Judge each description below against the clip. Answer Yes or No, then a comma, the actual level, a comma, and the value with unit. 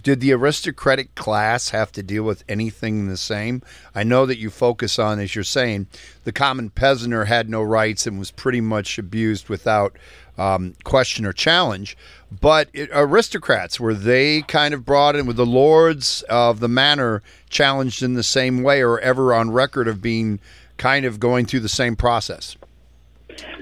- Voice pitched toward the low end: Yes, low, 120 Hz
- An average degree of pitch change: Yes, average, 3.8 semitones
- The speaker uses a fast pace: No, average, 175 wpm